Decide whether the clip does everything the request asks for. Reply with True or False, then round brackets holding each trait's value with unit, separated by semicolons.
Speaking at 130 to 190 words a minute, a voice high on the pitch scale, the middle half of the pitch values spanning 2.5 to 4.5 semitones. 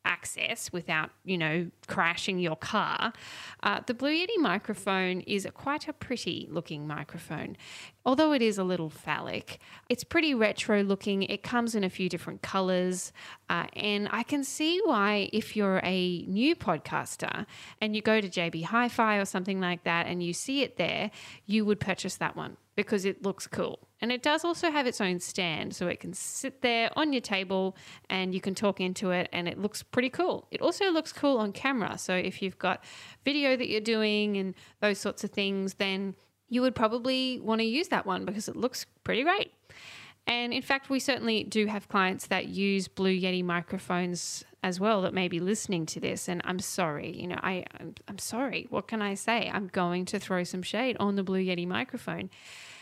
False (200 wpm; 195 Hz; 4.2 semitones)